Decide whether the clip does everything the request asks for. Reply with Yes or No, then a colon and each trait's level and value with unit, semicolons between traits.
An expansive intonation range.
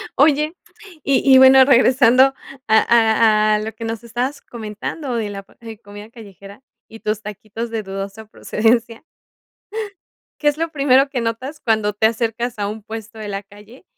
No: average, 3.1 semitones